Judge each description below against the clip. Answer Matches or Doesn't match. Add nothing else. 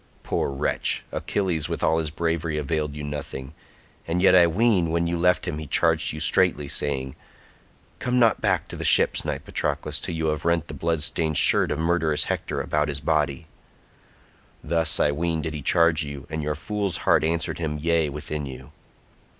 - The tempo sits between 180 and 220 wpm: Matches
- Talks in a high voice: Doesn't match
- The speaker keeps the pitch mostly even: Matches